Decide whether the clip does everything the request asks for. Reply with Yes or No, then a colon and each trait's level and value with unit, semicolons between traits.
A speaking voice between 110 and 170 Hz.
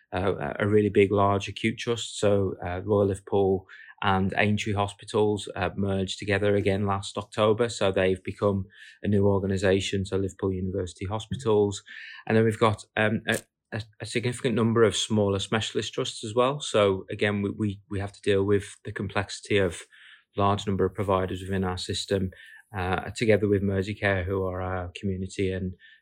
No: low, 100 Hz